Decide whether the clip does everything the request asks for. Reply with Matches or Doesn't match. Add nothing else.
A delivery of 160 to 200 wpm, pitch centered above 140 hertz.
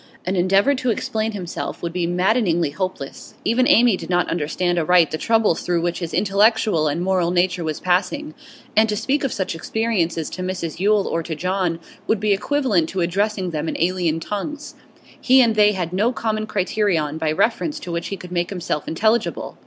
Matches